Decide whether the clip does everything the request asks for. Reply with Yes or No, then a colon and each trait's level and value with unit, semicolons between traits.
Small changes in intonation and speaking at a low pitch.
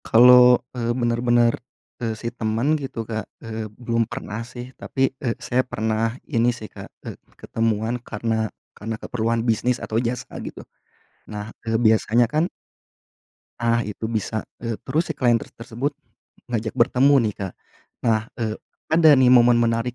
Yes: narrow, 1.7 semitones; low, 115 Hz